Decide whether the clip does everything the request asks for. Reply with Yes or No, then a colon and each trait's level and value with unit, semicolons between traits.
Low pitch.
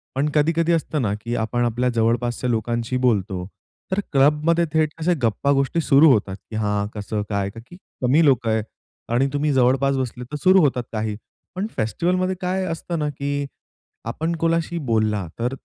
Yes: low, 130 Hz